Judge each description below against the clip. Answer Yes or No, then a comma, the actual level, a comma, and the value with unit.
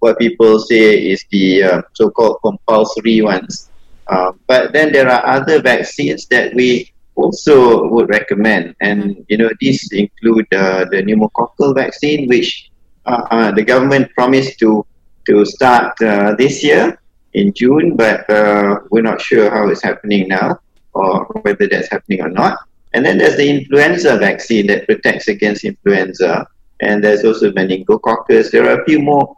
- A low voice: Yes, low, 110 Hz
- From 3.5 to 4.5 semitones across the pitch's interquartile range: Yes, average, 4.1 semitones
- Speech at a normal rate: Yes, average, 160 wpm